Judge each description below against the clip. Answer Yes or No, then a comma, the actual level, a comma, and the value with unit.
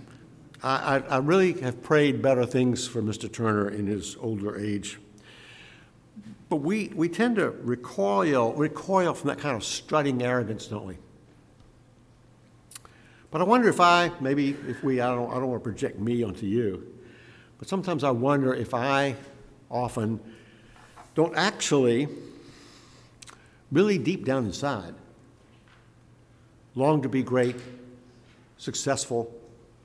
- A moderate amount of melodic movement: Yes, average, 3.5 semitones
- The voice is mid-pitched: No, low, 125 Hz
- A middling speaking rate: No, slow, 130 wpm